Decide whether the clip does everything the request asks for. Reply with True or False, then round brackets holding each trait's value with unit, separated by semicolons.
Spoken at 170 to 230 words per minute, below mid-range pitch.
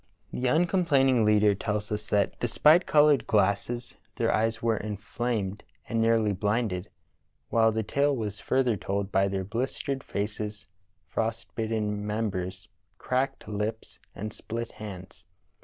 False (140 wpm; 110 Hz)